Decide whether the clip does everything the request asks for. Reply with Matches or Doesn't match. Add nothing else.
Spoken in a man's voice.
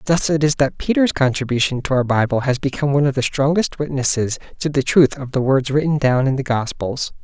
Matches